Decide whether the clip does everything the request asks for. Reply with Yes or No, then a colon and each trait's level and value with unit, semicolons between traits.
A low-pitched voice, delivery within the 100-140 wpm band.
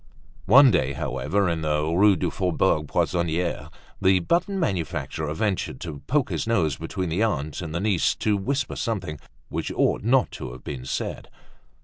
No: very low, 85 Hz; average, 170 wpm